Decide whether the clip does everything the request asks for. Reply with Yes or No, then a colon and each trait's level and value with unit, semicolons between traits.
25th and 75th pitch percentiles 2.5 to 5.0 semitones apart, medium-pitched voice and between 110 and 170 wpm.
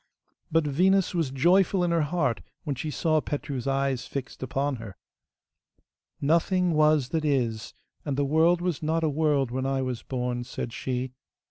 Yes: average, 3.8 semitones; medium, 145 Hz; average, 165 wpm